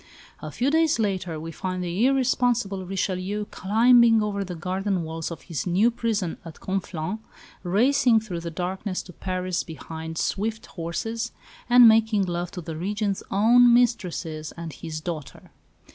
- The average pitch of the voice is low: No, high, 190 Hz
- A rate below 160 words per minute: Yes, average, 150 wpm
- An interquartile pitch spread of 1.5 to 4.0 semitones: No, average, 4.6 semitones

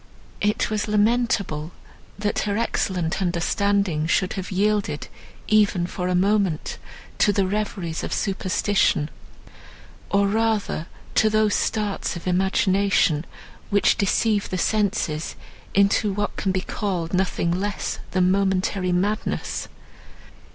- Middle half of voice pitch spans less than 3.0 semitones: Yes, narrow, 2.4 semitones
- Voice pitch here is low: No, high, 195 Hz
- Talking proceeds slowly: Yes, slow, 115 wpm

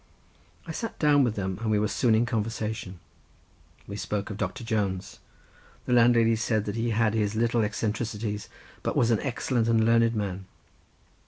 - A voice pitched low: Yes, low, 110 Hz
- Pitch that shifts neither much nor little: No, narrow, 1.9 semitones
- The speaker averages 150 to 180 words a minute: Yes, average, 165 wpm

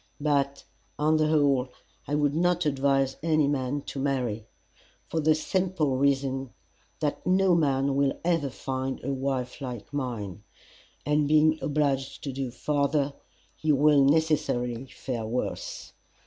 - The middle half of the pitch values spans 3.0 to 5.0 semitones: No, narrow, 2.4 semitones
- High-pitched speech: No, medium, 140 Hz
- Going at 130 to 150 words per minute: Yes, slow, 135 wpm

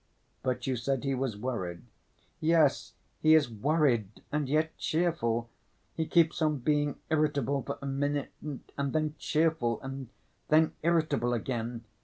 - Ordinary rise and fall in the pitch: Yes, average, 4.2 semitones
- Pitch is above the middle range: No, medium, 140 Hz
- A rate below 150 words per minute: Yes, average, 140 wpm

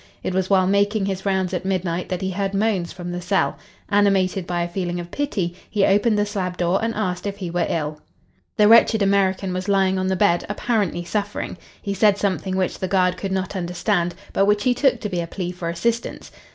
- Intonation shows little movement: Yes, narrow, 2.2 semitones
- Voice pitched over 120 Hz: Yes, high, 190 Hz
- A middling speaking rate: No, fast, 220 wpm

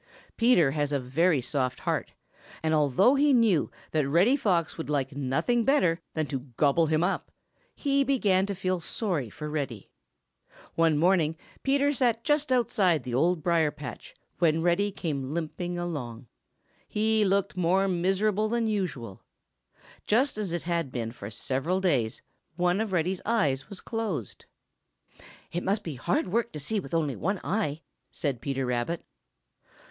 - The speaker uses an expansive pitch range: Yes, wide, 6.0 semitones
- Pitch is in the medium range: Yes, medium, 170 Hz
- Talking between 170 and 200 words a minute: No, average, 155 wpm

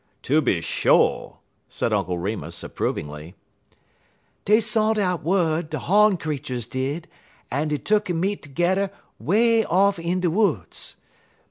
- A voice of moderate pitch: Yes, medium, 170 Hz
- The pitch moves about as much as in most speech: No, wide, 7.4 semitones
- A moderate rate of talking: No, slow, 125 wpm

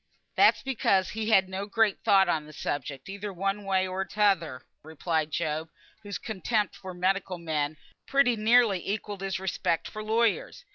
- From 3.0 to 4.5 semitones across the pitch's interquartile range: Yes, average, 3.9 semitones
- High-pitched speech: Yes, high, 195 Hz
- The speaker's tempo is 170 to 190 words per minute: No, average, 160 wpm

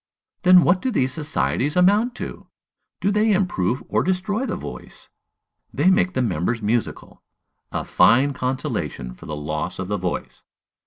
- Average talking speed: Yes, average, 155 wpm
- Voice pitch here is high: No, medium, 140 Hz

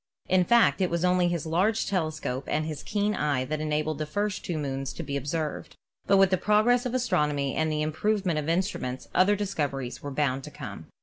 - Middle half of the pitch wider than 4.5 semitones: Yes, average, 4.9 semitones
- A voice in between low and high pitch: Yes, medium, 160 Hz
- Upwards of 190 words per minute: Yes, fast, 205 wpm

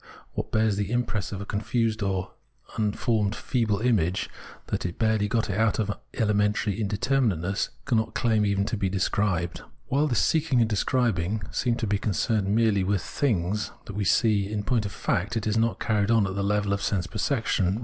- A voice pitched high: No, low, 105 Hz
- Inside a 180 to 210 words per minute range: Yes, average, 190 wpm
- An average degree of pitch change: No, narrow, 2.3 semitones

